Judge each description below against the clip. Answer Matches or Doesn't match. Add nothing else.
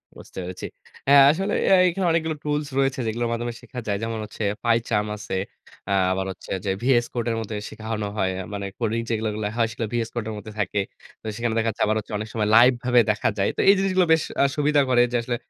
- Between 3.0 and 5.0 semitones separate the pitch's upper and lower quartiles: Matches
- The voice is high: Doesn't match